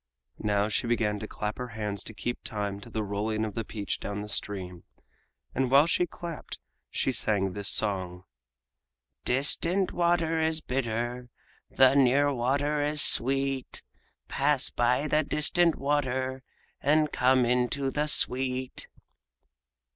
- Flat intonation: No, average, 5.0 semitones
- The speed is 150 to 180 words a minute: No, slow, 135 wpm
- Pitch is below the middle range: Yes, low, 125 Hz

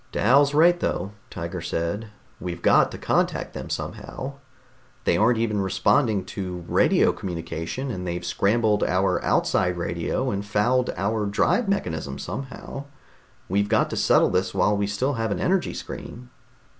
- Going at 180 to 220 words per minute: No, average, 150 wpm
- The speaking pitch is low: Yes, low, 100 Hz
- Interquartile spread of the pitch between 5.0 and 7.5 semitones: Yes, wide, 5.5 semitones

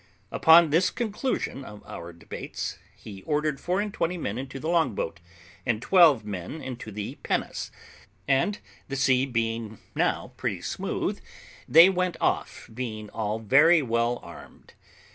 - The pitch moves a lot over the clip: Yes, wide, 6.9 semitones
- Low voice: Yes, low, 130 Hz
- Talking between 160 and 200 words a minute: No, average, 145 wpm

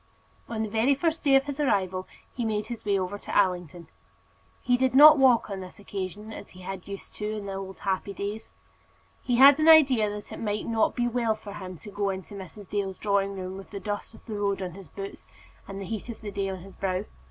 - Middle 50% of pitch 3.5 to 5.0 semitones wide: No, average, 2.9 semitones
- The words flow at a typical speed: No, fast, 245 wpm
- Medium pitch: No, high, 205 Hz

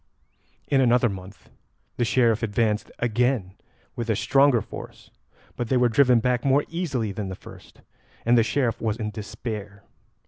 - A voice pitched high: No, low, 115 Hz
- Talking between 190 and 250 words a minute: No, average, 160 wpm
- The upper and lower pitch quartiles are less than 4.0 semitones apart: Yes, average, 2.9 semitones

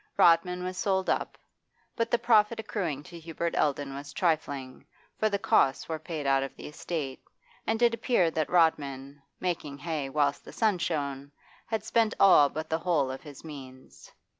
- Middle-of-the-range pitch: Yes, medium, 160 Hz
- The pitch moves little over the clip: No, average, 4.6 semitones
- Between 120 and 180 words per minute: Yes, average, 175 wpm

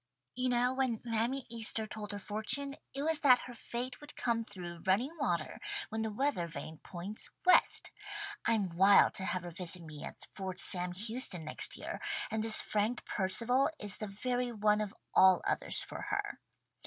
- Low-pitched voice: No, high, 215 Hz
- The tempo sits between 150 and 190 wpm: Yes, average, 180 wpm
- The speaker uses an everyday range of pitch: Yes, average, 4.7 semitones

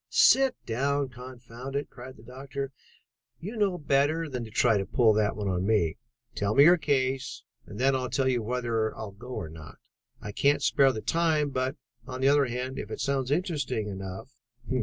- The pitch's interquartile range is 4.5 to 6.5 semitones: No, average, 4.1 semitones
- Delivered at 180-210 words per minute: Yes, average, 190 wpm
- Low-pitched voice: Yes, low, 130 Hz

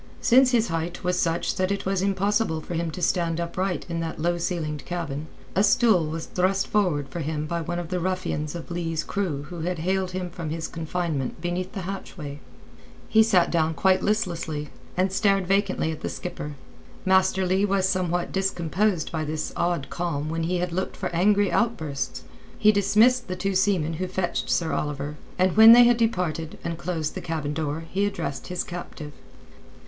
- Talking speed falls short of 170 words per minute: No, average, 190 wpm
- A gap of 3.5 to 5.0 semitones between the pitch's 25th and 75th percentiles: No, average, 3.0 semitones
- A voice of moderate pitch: Yes, medium, 175 Hz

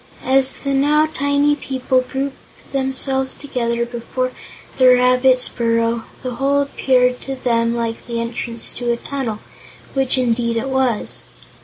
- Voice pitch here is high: Yes, very high, 255 Hz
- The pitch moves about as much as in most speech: No, narrow, 2.3 semitones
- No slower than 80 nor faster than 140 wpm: Yes, slow, 135 wpm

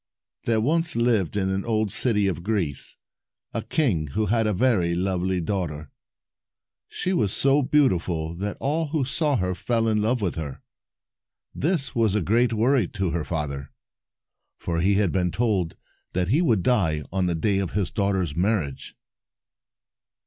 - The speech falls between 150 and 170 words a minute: Yes, average, 165 wpm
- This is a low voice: Yes, low, 100 Hz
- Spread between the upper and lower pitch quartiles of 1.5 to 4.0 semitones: No, average, 5.1 semitones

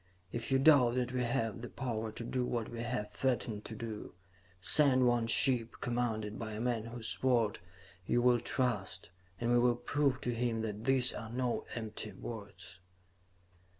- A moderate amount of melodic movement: No, narrow, 1.9 semitones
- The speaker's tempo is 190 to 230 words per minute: No, average, 175 wpm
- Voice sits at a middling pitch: No, low, 120 Hz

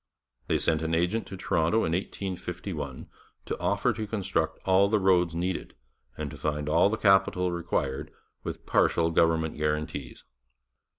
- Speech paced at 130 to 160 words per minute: Yes, average, 145 wpm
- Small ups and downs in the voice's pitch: No, average, 3.6 semitones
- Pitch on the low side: Yes, very low, 85 Hz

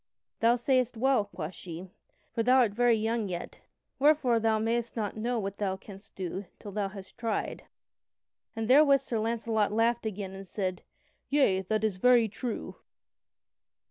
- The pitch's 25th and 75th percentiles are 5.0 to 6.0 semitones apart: No, average, 3.3 semitones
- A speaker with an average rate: Yes, average, 160 wpm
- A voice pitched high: Yes, high, 220 Hz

